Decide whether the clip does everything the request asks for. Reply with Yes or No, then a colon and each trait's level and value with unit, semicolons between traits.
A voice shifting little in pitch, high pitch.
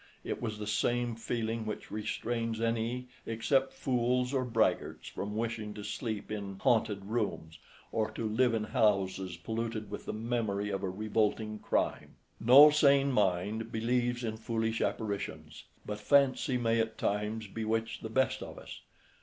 No: narrow, 2.2 semitones; low, 110 Hz